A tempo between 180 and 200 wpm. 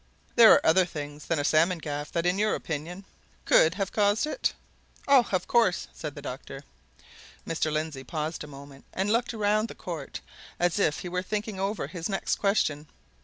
Yes: average, 185 wpm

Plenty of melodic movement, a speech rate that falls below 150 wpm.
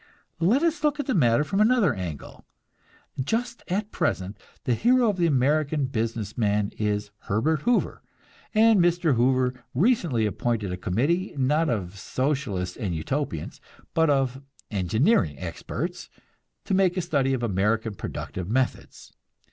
Yes: wide, 8.8 semitones; average, 140 wpm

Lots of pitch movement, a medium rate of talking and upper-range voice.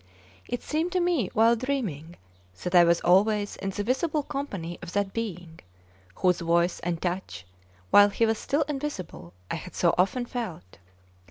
Yes: wide, 6.6 semitones; average, 165 wpm; high, 200 Hz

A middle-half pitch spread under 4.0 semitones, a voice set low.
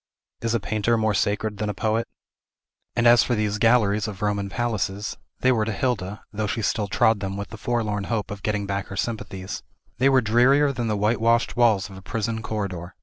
Yes: narrow, 2.4 semitones; low, 110 Hz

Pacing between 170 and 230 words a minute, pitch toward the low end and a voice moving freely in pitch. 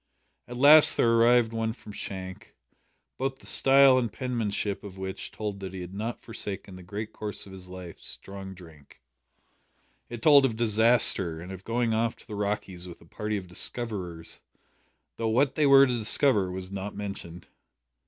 No: average, 175 wpm; low, 105 Hz; average, 4.0 semitones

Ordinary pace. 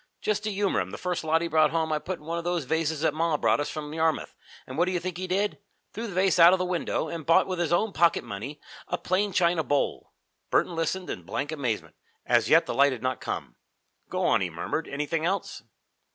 No: fast, 245 wpm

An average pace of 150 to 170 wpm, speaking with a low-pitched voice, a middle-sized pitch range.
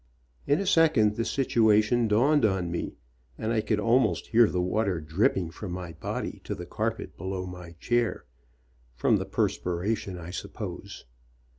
Yes: average, 165 wpm; low, 105 Hz; average, 4.5 semitones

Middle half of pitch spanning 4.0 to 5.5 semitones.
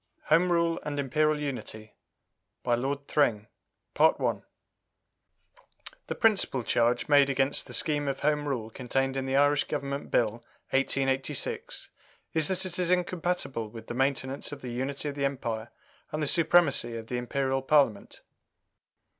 No: average, 3.2 semitones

